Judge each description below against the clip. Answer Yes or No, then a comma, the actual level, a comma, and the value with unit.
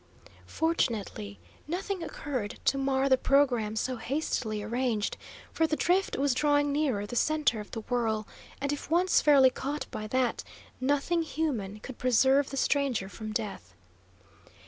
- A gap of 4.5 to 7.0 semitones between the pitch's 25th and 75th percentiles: Yes, average, 4.9 semitones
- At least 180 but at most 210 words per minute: No, average, 145 wpm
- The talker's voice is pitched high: Yes, very high, 265 Hz